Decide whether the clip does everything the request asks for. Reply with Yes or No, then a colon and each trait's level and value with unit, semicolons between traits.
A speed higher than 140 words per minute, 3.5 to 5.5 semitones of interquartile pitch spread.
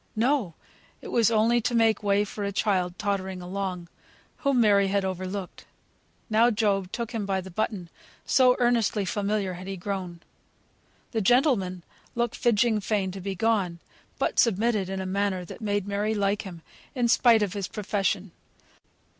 No: average, 165 wpm; average, 2.9 semitones